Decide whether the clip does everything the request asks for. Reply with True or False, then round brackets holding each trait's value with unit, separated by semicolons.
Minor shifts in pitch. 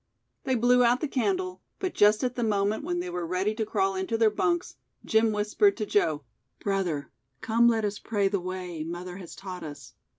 False (4.3 semitones)